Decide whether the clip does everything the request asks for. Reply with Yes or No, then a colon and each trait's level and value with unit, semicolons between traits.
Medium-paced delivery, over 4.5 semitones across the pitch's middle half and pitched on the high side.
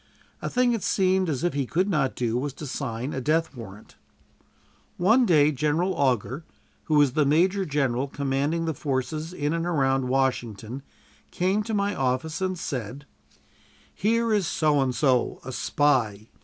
No: average, 165 wpm; average, 5.0 semitones; medium, 145 Hz